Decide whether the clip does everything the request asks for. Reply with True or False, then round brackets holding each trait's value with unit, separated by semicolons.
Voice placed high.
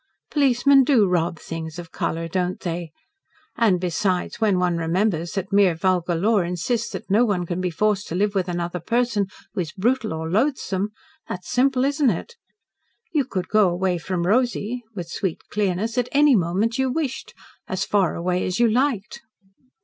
True (195 Hz)